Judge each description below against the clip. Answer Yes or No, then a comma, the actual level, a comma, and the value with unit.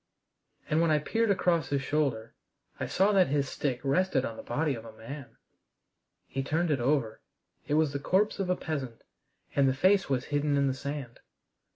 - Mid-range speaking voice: Yes, medium, 145 Hz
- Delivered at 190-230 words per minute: Yes, average, 195 wpm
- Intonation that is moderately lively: Yes, average, 3.7 semitones